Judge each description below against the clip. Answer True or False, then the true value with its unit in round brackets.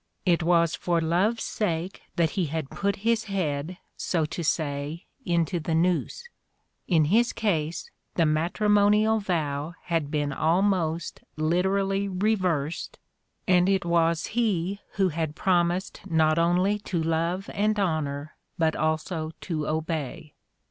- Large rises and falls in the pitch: False (3.6 semitones)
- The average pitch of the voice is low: False (170 Hz)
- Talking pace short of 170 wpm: True (135 wpm)